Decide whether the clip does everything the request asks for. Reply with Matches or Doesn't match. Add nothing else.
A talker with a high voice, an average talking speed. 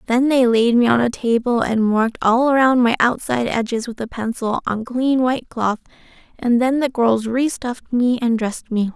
Doesn't match